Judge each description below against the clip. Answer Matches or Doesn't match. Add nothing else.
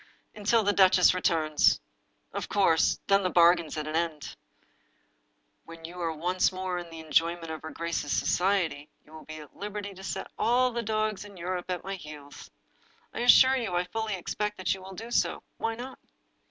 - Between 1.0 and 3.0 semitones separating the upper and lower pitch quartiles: Doesn't match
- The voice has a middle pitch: Matches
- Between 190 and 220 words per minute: Matches